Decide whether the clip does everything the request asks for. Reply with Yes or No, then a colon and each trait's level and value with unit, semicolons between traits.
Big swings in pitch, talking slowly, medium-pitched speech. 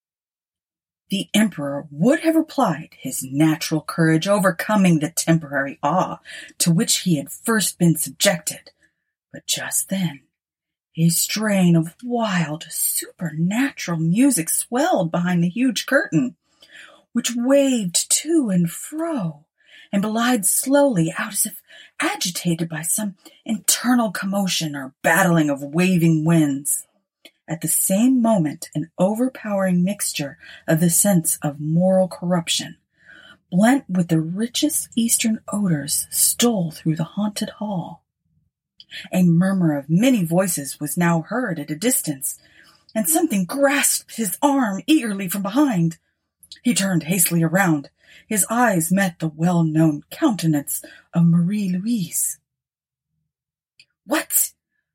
Yes: wide, 5.7 semitones; slow, 120 wpm; medium, 180 Hz